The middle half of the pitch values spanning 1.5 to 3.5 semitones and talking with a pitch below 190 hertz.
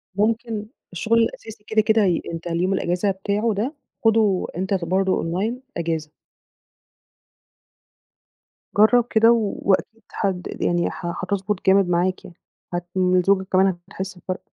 No: average, 3.2 semitones; high, 195 Hz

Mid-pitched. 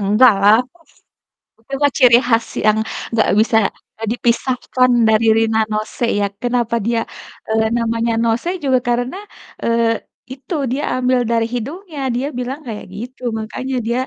No: high, 235 Hz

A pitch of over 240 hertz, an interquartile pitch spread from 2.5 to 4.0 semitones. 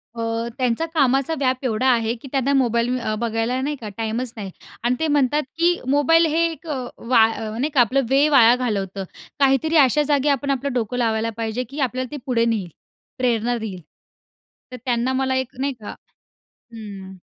Yes: very high, 250 Hz; average, 3.4 semitones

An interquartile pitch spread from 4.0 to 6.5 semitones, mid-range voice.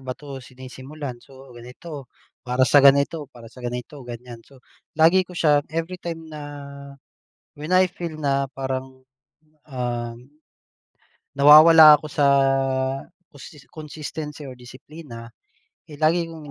No: average, 3.4 semitones; medium, 145 Hz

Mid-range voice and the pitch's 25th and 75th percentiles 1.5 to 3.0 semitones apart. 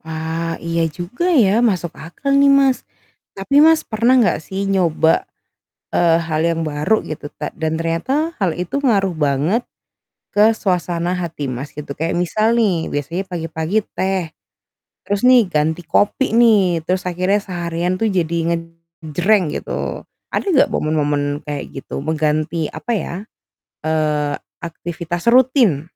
No: medium, 175 Hz; average, 4.9 semitones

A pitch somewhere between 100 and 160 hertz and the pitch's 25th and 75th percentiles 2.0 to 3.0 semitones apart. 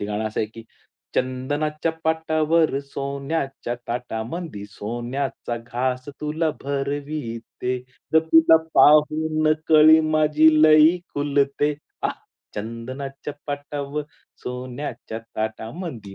No: medium, 140 Hz; average, 4.0 semitones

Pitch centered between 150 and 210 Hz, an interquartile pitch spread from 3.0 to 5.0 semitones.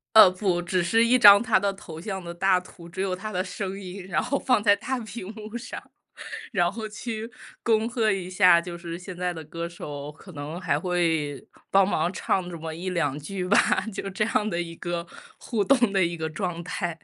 Yes: medium, 185 Hz; average, 3.4 semitones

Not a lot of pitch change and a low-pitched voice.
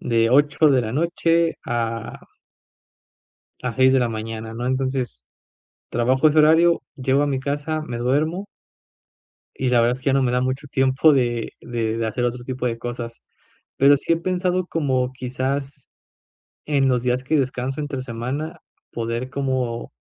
No: average, 3.0 semitones; low, 130 Hz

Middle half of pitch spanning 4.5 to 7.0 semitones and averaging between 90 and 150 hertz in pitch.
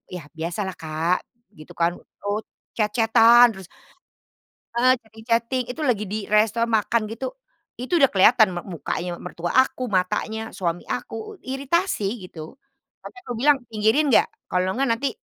No: average, 5.3 semitones; high, 220 Hz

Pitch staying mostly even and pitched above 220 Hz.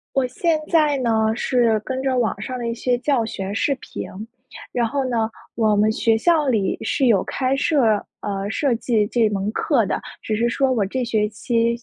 No: average, 3.3 semitones; high, 235 Hz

